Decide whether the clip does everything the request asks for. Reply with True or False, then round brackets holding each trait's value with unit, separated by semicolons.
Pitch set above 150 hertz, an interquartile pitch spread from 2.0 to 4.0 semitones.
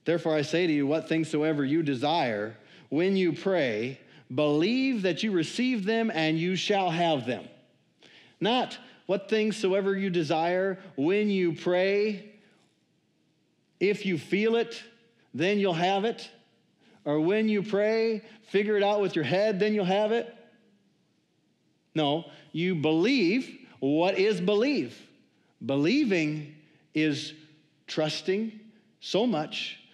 False (185 Hz; 5.2 semitones)